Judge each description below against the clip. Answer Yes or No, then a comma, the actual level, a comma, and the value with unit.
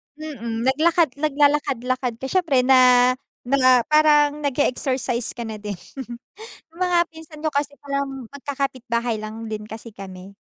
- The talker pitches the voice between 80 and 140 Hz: No, very high, 265 Hz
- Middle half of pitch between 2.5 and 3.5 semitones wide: No, average, 3.9 semitones